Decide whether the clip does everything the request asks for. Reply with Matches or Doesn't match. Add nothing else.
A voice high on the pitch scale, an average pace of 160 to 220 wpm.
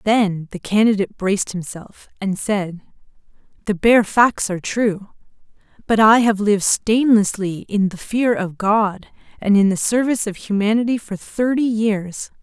Doesn't match